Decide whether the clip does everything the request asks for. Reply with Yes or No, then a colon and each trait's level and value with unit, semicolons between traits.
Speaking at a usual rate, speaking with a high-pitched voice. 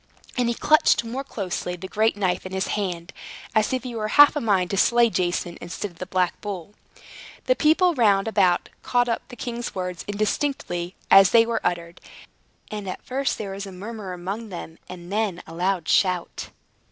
Yes: average, 190 wpm; high, 200 Hz